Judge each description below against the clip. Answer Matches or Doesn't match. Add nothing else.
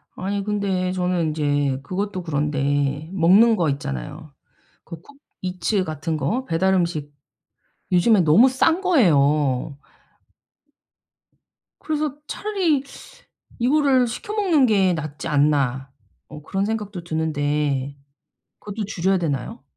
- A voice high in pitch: Doesn't match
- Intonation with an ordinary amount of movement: Doesn't match